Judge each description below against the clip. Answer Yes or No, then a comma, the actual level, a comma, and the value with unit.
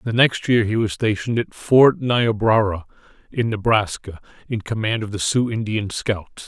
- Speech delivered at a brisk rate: No, average, 165 wpm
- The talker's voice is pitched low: Yes, low, 110 Hz